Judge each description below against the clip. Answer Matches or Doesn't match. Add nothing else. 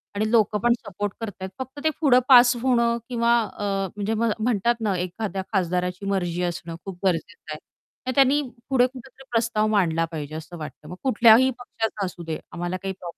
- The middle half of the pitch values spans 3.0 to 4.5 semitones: Doesn't match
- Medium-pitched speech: Doesn't match